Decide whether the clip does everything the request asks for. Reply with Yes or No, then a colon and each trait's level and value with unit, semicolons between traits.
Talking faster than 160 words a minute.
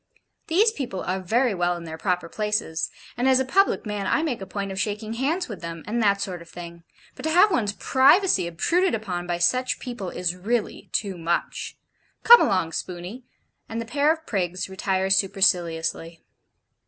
Yes: average, 185 wpm